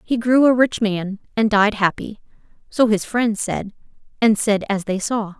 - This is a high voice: Yes, high, 215 Hz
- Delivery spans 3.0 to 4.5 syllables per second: Yes, 4.4 syllables/s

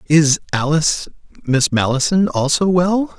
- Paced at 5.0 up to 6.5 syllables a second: No, 4.4 syllables/s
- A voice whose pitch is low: No, medium, 160 Hz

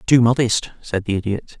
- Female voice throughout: No, male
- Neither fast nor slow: Yes, average, 190 wpm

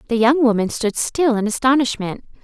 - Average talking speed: Yes, average, 170 wpm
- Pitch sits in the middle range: No, high, 240 Hz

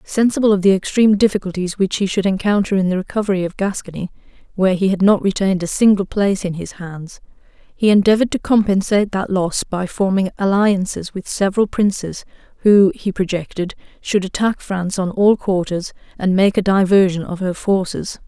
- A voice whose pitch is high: Yes, high, 195 Hz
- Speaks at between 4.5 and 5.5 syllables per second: No, 5.7 syllables/s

